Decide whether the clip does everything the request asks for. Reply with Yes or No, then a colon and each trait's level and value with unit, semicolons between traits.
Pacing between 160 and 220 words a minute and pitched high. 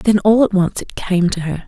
No: fast, 285 wpm; high, 195 Hz